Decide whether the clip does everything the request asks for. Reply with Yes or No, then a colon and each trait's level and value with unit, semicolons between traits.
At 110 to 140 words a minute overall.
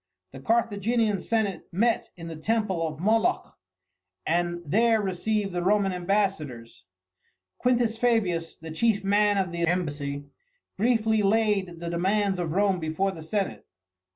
Yes: slow, 135 wpm